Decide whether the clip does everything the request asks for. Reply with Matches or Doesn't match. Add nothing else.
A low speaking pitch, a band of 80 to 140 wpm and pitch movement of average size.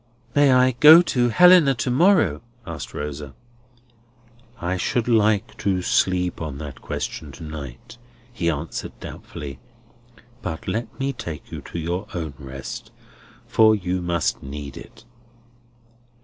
Doesn't match